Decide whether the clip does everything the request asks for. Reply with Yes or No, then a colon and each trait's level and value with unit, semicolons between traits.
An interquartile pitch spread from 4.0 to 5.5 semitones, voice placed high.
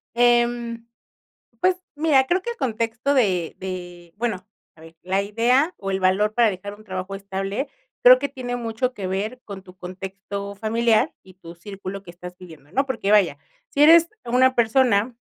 Yes: average, 4.5 semitones; high, 210 Hz